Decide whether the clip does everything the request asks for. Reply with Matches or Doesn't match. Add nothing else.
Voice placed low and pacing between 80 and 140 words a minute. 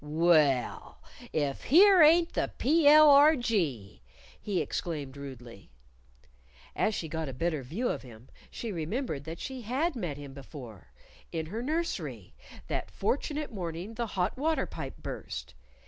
Doesn't match